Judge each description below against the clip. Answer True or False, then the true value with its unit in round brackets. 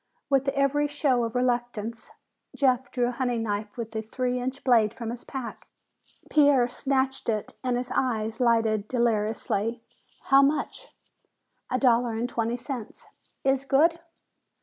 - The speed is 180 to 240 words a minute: False (145 wpm)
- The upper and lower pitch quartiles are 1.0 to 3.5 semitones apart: True (2.9 semitones)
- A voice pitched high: True (245 Hz)